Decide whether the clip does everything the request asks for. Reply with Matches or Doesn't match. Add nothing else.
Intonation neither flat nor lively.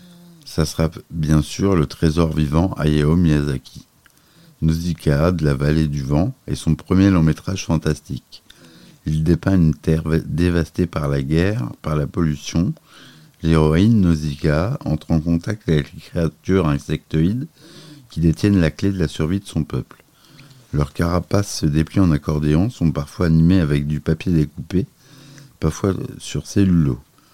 Matches